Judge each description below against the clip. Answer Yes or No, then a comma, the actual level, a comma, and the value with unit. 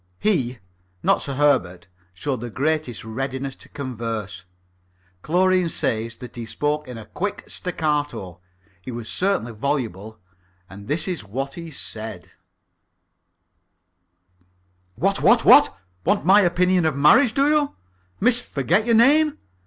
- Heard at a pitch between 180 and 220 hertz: No, medium, 140 Hz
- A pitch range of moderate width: No, wide, 8.1 semitones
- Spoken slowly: Yes, slow, 130 wpm